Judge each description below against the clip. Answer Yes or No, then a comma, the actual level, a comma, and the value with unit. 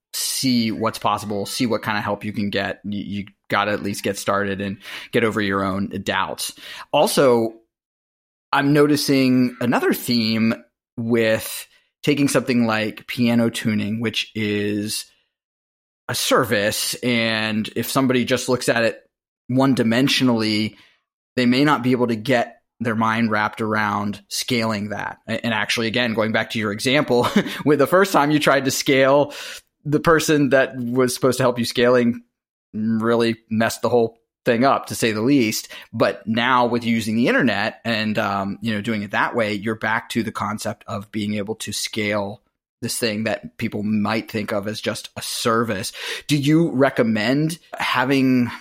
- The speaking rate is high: No, average, 170 wpm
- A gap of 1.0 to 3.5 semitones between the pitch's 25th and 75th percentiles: Yes, average, 2.9 semitones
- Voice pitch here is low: Yes, low, 115 Hz